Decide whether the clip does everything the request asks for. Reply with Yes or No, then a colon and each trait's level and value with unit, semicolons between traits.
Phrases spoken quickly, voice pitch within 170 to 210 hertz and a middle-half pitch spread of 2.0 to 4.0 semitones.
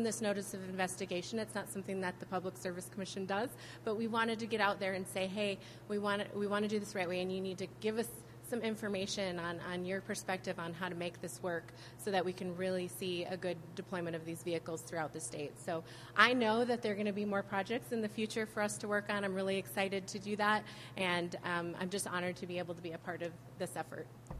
Yes: fast, 260 wpm; high, 190 Hz; average, 2.7 semitones